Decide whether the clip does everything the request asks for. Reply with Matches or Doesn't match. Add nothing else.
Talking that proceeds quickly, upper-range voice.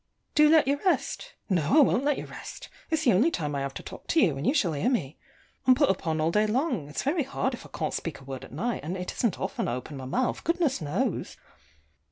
Matches